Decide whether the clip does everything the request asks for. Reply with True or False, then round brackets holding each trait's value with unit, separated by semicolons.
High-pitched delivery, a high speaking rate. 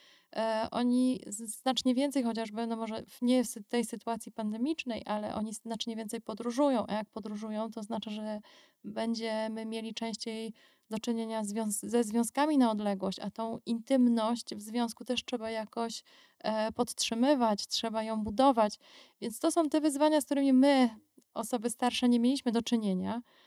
False (230 Hz; 145 wpm)